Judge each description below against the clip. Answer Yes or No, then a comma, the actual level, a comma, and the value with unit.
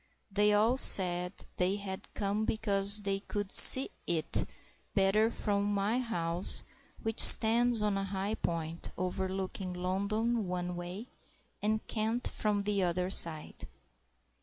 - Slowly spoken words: Yes, slow, 130 wpm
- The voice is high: Yes, high, 200 Hz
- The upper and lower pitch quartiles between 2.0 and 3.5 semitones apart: Yes, average, 2.8 semitones